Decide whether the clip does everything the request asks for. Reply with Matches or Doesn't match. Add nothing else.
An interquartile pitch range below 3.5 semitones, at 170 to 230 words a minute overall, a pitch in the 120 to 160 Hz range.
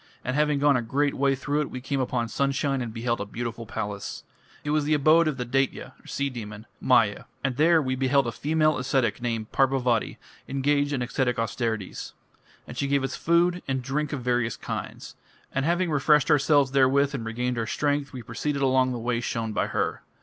Matches